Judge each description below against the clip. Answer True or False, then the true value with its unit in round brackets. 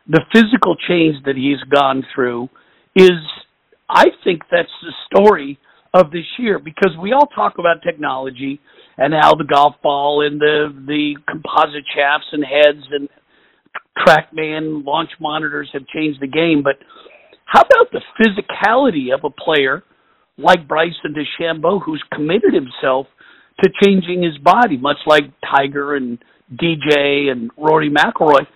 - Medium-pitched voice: True (150 Hz)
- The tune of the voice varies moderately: True (3.7 semitones)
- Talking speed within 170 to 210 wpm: False (145 wpm)